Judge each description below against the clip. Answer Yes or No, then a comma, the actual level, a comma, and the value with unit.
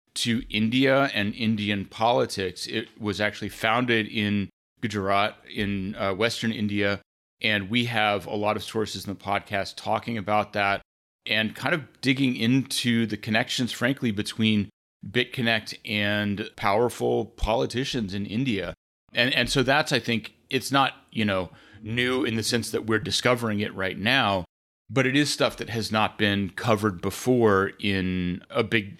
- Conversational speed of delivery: Yes, average, 155 wpm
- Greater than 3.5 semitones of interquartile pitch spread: No, average, 3.0 semitones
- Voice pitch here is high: No, low, 110 Hz